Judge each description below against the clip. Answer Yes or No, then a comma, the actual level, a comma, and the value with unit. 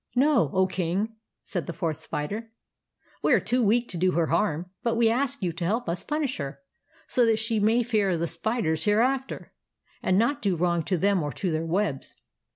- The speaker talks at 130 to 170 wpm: No, fast, 205 wpm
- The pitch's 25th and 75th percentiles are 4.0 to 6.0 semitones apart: Yes, wide, 5.5 semitones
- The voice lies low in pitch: No, high, 200 Hz